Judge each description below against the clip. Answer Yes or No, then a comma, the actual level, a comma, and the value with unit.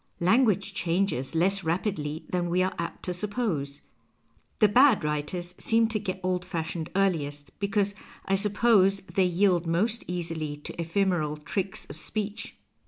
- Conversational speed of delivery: Yes, average, 150 wpm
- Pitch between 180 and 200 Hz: Yes, medium, 185 Hz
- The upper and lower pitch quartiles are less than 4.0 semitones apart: Yes, average, 3.5 semitones